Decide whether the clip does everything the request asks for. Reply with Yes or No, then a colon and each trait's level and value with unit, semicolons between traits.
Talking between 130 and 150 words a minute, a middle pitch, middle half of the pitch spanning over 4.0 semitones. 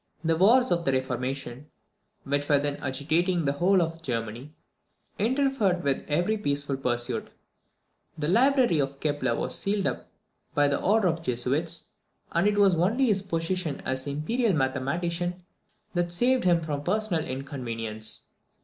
Yes: average, 145 wpm; medium, 160 Hz; wide, 5.5 semitones